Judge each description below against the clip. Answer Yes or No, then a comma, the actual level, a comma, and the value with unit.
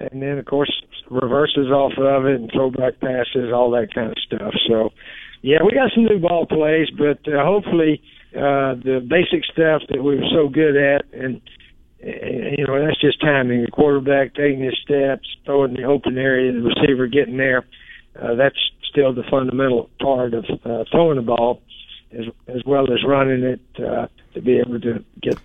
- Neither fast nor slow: Yes, average, 190 wpm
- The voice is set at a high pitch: No, low, 135 Hz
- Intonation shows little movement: Yes, narrow, 2.3 semitones